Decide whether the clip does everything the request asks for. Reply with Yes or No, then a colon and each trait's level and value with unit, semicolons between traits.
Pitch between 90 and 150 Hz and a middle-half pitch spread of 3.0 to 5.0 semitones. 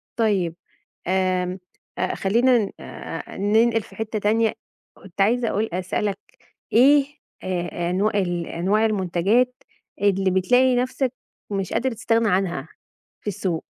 No: high, 205 Hz; average, 3.7 semitones